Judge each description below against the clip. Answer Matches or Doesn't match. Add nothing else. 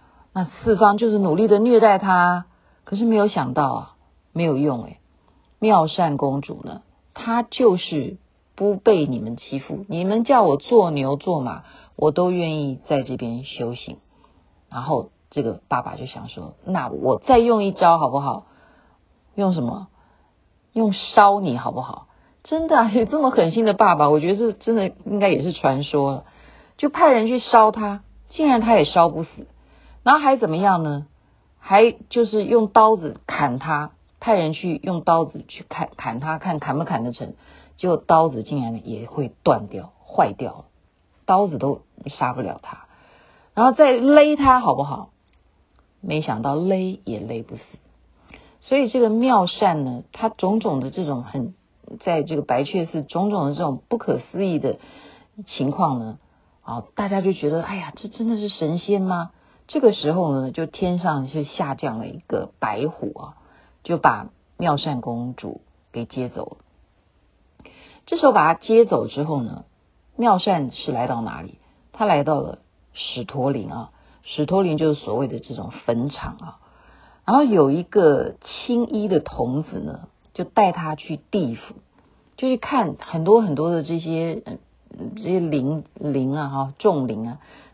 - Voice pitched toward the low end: Doesn't match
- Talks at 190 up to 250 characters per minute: Matches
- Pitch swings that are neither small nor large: Doesn't match